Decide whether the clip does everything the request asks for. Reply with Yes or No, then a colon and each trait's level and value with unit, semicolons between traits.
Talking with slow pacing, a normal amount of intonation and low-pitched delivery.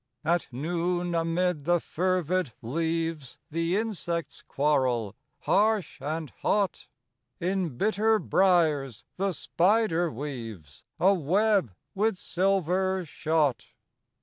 No: slow, 95 wpm; average, 4.3 semitones; medium, 170 Hz